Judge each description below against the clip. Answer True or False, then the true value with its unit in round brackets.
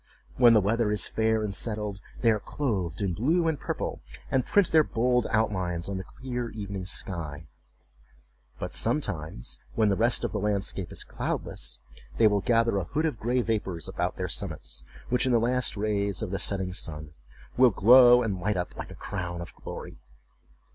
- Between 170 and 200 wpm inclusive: True (185 wpm)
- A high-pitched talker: False (105 Hz)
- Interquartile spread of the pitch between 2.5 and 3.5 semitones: False (4.3 semitones)